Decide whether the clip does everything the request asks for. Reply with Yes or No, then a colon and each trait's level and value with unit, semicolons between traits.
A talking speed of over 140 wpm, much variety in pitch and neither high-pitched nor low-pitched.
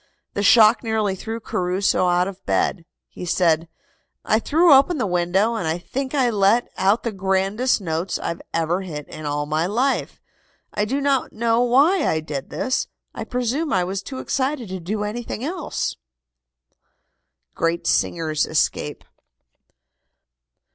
No: average, 150 wpm; wide, 5.8 semitones; high, 200 Hz